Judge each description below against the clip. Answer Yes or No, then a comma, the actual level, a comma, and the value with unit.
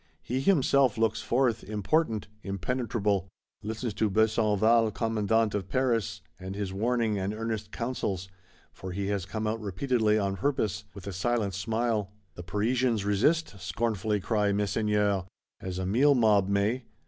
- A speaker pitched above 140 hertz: No, low, 105 Hz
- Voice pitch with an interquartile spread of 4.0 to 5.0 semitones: No, average, 2.7 semitones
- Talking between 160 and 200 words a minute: No, average, 145 wpm